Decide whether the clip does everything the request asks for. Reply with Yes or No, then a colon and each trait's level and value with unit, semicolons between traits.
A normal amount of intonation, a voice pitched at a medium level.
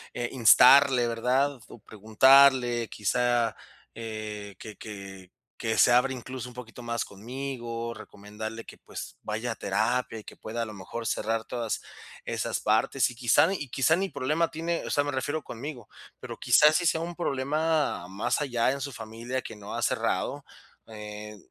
No: average, 3.7 semitones; low, 120 Hz